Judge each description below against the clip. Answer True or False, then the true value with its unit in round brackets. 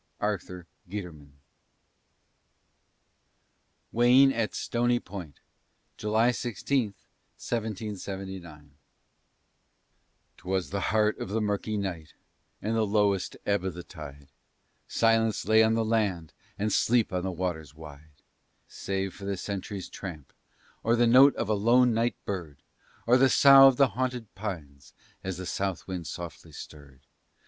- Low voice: True (100 Hz)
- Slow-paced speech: True (130 wpm)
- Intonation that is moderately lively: True (4.2 semitones)